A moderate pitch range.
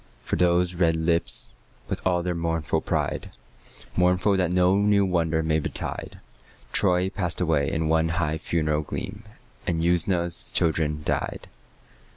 No: narrow, 2.0 semitones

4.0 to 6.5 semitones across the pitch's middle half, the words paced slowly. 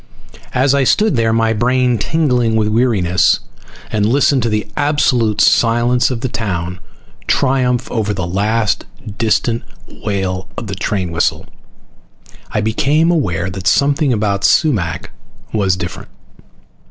Yes: average, 4.3 semitones; slow, 130 wpm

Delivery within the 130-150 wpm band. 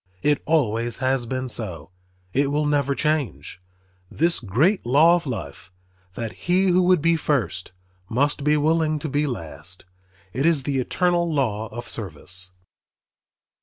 Yes: average, 145 wpm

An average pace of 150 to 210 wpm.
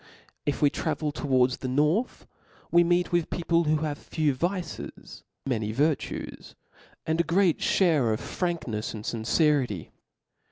No: slow, 135 wpm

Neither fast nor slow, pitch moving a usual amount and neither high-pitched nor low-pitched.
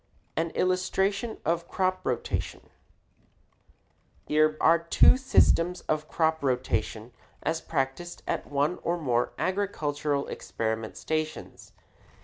No: slow, 105 wpm; average, 4.0 semitones; medium, 160 Hz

